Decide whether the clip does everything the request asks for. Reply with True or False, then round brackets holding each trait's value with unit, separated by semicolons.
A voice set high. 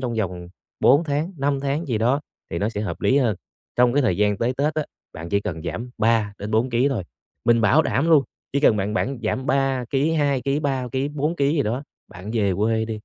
False (125 Hz)